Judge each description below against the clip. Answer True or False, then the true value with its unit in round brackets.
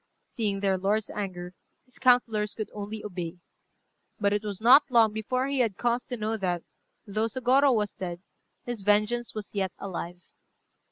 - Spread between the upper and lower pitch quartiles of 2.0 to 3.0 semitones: False (3.4 semitones)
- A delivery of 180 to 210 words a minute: False (165 wpm)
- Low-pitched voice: False (215 Hz)